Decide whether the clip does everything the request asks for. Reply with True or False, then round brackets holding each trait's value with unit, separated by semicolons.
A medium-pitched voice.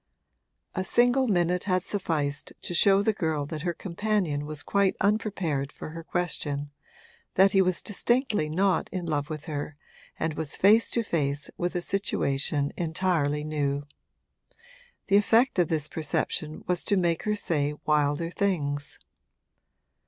True (170 Hz)